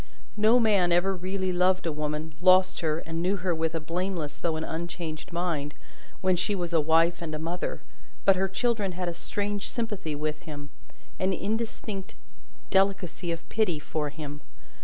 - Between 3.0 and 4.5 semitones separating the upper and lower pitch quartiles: Yes, average, 3.3 semitones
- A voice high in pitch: No, medium, 175 Hz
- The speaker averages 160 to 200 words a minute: Yes, average, 175 wpm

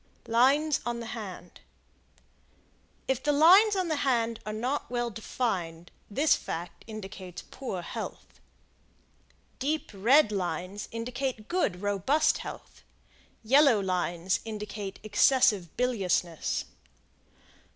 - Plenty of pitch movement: Yes, wide, 6.0 semitones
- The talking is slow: Yes, slow, 105 wpm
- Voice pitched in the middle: No, high, 225 Hz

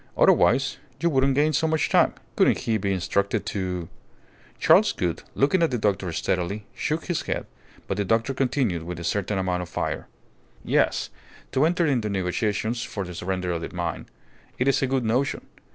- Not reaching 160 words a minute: No, average, 185 wpm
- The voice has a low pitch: Yes, low, 105 Hz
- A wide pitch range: Yes, wide, 6.6 semitones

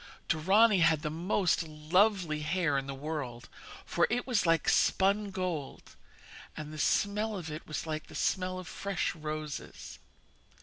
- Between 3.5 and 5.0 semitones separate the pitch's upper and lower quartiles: Yes, average, 4.0 semitones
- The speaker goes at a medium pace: Yes, average, 150 wpm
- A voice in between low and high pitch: Yes, medium, 165 Hz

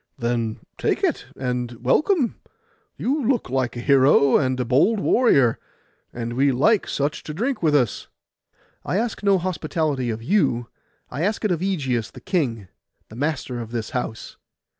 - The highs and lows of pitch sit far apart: Yes, wide, 7.5 semitones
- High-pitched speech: No, low, 135 Hz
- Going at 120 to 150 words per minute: No, average, 160 wpm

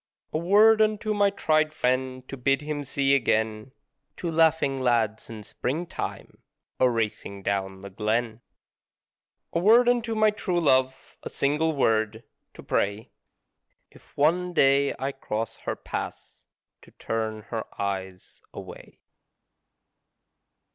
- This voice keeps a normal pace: No, slow, 125 wpm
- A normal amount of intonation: No, wide, 6.9 semitones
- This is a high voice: No, low, 135 Hz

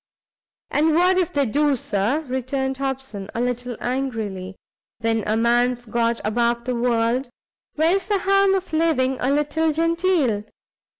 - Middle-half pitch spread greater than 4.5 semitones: Yes, average, 5.1 semitones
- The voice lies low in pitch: No, very high, 260 Hz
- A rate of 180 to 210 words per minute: No, average, 140 wpm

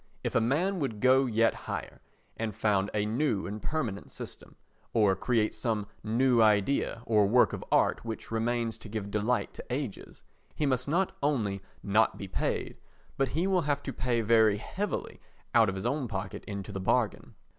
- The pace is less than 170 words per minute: No, average, 175 wpm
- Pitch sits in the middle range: No, low, 115 Hz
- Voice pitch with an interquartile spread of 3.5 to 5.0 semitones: Yes, average, 4.1 semitones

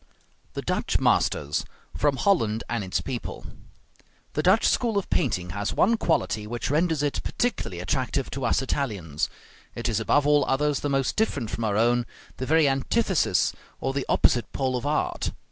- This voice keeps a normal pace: Yes, average, 170 wpm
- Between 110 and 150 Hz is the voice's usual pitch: Yes, low, 135 Hz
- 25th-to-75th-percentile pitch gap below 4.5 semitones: No, average, 4.8 semitones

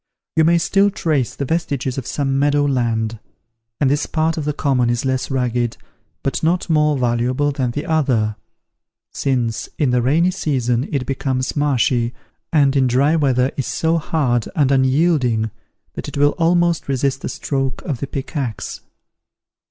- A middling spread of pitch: Yes, average, 3.2 semitones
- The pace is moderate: Yes, average, 160 wpm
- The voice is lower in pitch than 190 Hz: Yes, low, 135 Hz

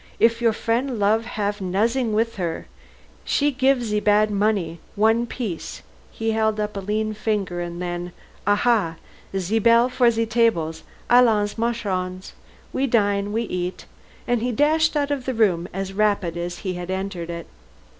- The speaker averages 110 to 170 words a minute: Yes, average, 165 wpm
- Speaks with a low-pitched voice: No, high, 210 Hz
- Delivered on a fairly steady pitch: No, average, 3.8 semitones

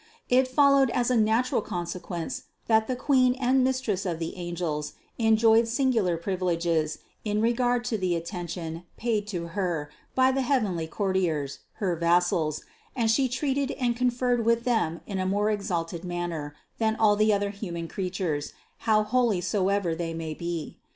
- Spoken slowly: No, average, 165 wpm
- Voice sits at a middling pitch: No, high, 200 Hz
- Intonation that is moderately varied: No, wide, 5.7 semitones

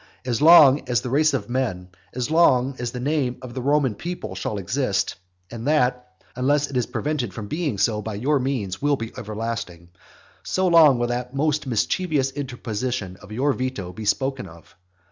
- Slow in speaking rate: No, average, 185 wpm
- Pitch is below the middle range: Yes, low, 125 Hz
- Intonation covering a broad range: No, average, 4.3 semitones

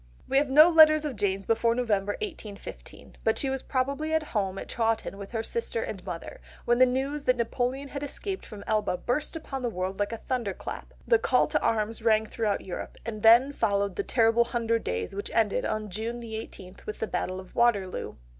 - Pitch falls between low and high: No, high, 230 Hz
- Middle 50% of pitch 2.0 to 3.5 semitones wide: No, average, 4.6 semitones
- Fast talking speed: Yes, fast, 210 wpm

